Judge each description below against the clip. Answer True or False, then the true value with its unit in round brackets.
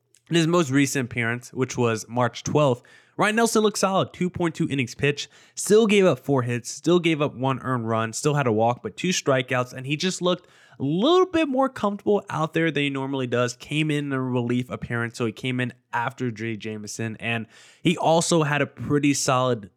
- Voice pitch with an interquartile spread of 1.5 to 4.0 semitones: False (5.6 semitones)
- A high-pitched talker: False (140 Hz)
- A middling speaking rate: False (210 wpm)